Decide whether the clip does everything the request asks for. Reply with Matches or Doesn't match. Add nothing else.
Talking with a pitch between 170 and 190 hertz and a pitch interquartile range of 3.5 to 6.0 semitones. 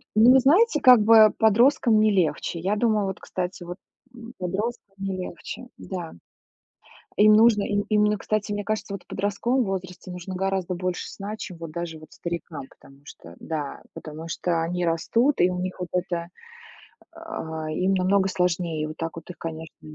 Matches